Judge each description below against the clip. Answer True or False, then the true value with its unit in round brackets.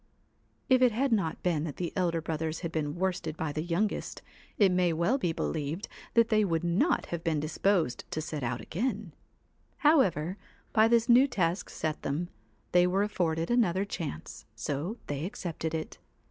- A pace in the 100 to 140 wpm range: False (170 wpm)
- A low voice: False (175 Hz)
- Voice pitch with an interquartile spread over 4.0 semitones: True (4.7 semitones)